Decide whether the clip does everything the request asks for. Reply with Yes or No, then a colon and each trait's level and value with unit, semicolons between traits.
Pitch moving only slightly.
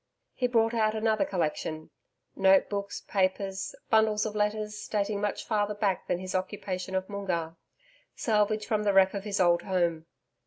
Yes: narrow, 2.2 semitones